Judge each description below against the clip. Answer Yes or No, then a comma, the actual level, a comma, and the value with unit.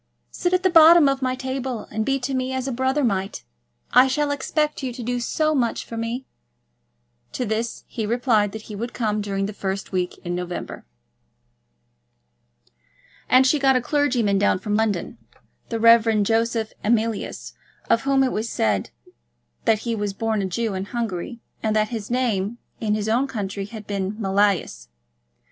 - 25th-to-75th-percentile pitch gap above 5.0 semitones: No, average, 3.9 semitones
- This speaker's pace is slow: No, average, 180 wpm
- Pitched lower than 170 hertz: No, high, 230 Hz